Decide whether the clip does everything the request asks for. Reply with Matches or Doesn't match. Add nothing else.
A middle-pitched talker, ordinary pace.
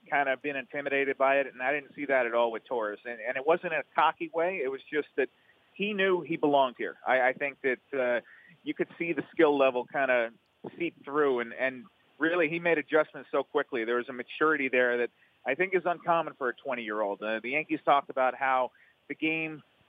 Doesn't match